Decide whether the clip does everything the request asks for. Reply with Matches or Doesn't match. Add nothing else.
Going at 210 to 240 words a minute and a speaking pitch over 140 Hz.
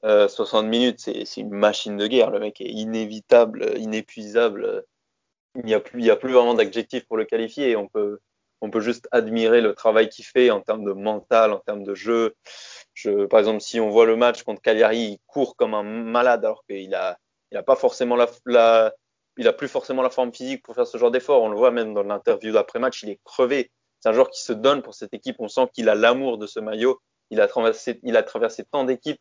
Doesn't match